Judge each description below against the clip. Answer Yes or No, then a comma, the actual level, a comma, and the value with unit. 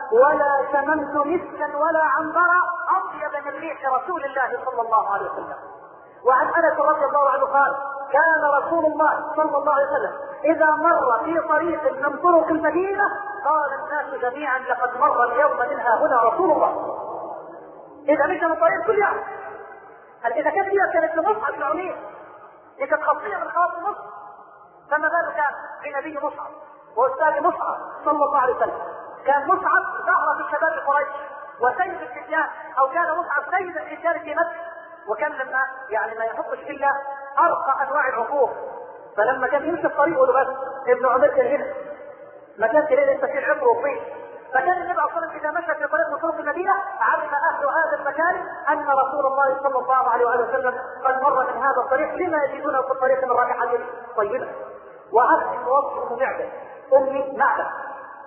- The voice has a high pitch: Yes, very high, 290 Hz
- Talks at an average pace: No, fast, 150 wpm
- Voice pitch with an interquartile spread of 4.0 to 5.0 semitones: No, average, 3.3 semitones